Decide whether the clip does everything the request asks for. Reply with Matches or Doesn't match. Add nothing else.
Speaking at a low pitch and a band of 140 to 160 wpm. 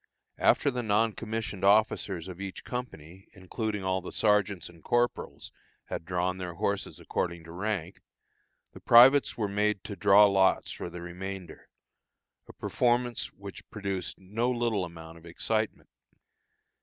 Matches